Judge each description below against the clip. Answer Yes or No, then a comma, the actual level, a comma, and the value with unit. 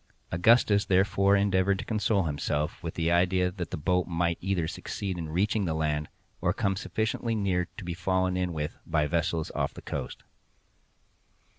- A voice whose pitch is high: No, very low, 90 Hz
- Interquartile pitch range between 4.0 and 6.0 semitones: No, average, 2.9 semitones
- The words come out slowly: No, average, 170 wpm